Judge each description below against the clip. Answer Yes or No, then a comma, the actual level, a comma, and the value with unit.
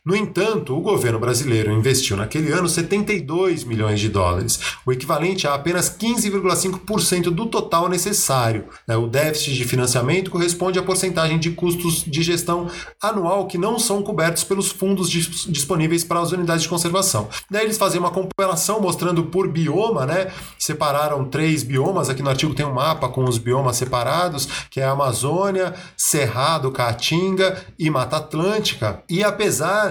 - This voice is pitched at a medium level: Yes, medium, 170 Hz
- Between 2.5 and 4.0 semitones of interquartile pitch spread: No, average, 5.3 semitones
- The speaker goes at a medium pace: Yes, average, 155 wpm